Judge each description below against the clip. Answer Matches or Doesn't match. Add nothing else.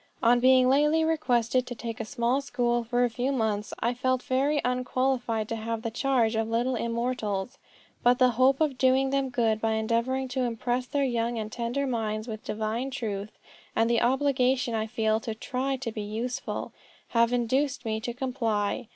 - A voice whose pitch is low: Doesn't match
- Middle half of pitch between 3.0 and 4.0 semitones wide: Doesn't match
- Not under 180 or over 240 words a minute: Matches